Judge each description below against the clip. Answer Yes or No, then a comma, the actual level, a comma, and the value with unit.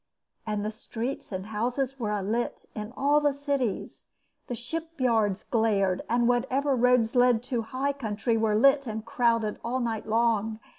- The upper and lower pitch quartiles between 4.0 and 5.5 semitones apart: No, average, 3.1 semitones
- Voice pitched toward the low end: No, high, 235 Hz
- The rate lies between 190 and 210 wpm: No, average, 155 wpm